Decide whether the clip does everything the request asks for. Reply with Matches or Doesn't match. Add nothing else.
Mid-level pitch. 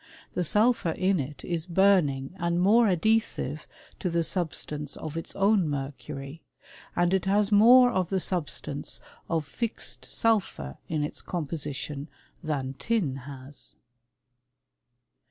Matches